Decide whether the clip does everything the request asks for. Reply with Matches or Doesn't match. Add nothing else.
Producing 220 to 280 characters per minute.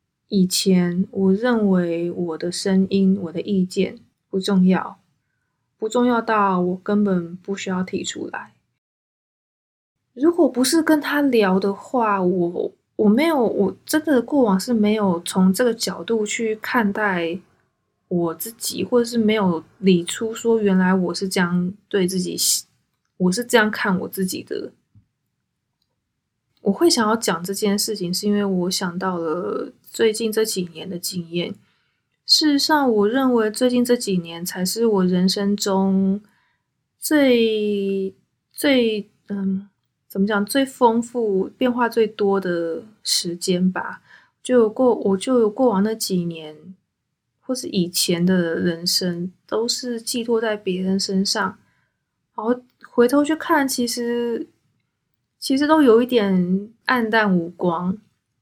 Doesn't match